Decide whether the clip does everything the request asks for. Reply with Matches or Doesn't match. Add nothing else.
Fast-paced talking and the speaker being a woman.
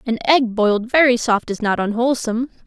Doesn't match